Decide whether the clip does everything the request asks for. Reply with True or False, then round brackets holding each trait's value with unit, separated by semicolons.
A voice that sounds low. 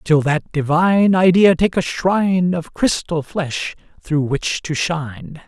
False (165 Hz)